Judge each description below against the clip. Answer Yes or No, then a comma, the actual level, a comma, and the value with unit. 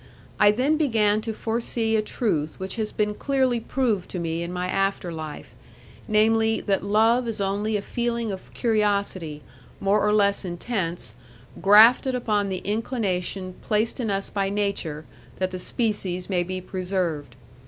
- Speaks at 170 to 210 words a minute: No, average, 155 wpm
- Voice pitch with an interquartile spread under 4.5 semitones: Yes, average, 3.2 semitones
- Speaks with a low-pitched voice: No, high, 205 Hz